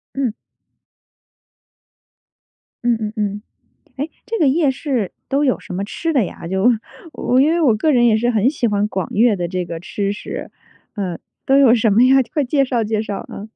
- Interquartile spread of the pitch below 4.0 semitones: No, average, 4.8 semitones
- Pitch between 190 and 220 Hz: No, high, 230 Hz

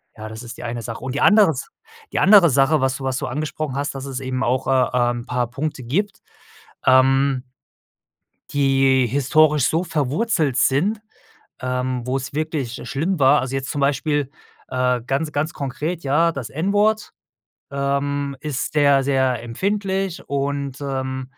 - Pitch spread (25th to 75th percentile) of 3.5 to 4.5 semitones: No, average, 2.9 semitones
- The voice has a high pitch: No, medium, 140 Hz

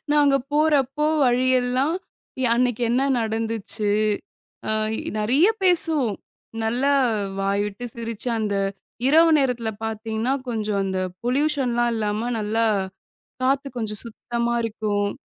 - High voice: Yes, high, 235 Hz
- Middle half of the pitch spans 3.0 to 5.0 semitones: Yes, average, 3.8 semitones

